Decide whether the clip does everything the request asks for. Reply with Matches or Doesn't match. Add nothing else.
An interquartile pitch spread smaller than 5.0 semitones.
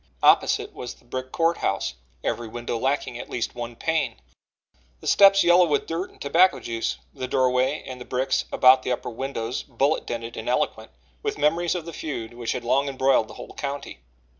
Matches